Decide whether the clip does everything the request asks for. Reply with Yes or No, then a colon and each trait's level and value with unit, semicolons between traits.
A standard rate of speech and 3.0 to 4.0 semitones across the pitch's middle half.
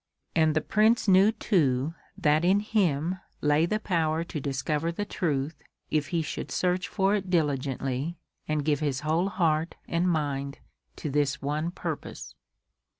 Yes: average, 150 wpm; average, 3.7 semitones